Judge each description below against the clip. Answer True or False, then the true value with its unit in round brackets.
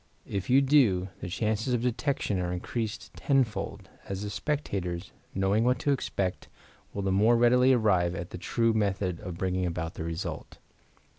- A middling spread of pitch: True (4.8 semitones)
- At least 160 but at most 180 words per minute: True (165 wpm)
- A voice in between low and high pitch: False (100 Hz)